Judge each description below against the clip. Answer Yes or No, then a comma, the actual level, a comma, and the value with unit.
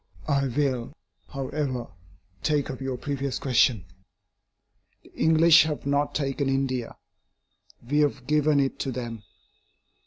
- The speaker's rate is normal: No, slow, 120 wpm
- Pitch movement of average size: No, narrow, 2.3 semitones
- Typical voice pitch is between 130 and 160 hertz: Yes, low, 135 Hz